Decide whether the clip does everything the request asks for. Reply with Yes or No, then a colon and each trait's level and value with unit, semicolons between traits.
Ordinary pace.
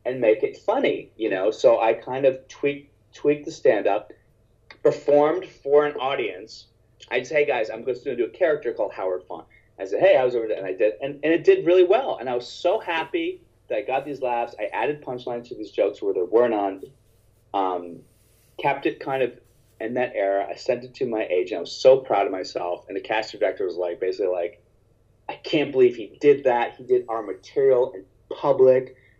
No: fast, 220 wpm